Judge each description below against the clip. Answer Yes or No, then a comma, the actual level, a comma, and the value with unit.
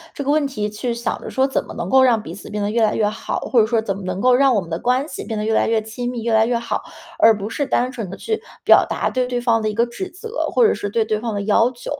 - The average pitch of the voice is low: No, high, 230 Hz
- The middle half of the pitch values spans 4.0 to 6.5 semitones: No, average, 3.0 semitones